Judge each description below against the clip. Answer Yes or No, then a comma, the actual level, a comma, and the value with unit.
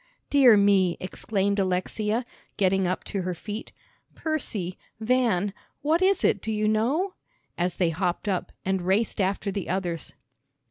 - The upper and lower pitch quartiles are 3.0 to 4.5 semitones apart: Yes, average, 3.3 semitones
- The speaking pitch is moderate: No, high, 200 Hz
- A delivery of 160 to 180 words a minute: No, average, 145 wpm